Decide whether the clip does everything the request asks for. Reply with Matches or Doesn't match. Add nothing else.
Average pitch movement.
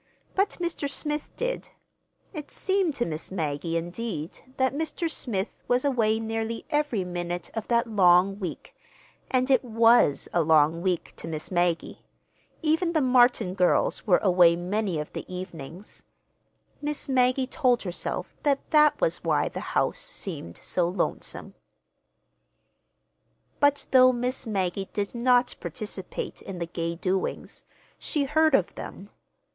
Doesn't match